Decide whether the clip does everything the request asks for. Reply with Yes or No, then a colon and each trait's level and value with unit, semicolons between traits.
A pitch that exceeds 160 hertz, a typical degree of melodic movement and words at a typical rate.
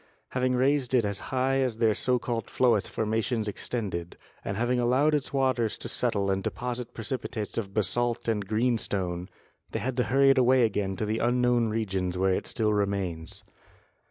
No: low, 115 Hz; average, 3.7 semitones; average, 180 wpm